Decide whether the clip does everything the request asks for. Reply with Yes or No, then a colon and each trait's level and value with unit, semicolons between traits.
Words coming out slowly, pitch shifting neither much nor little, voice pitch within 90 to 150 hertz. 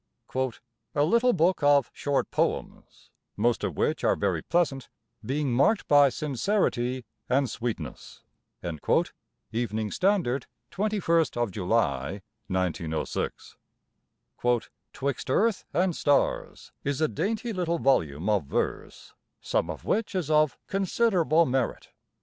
No: slow, 110 wpm; wide, 7.3 semitones; medium, 140 Hz